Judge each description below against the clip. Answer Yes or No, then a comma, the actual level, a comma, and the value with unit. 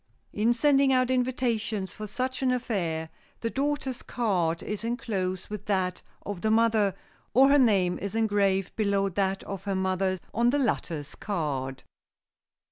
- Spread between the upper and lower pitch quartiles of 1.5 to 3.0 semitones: No, average, 4.4 semitones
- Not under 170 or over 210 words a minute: No, average, 150 wpm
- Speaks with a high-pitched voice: Yes, high, 210 Hz